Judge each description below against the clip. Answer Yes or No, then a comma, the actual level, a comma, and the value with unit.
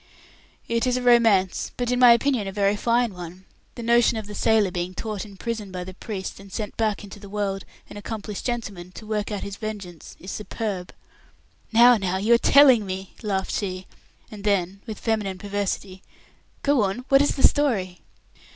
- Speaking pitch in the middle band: No, high, 205 Hz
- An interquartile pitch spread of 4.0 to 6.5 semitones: No, average, 3.3 semitones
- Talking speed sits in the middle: Yes, average, 190 wpm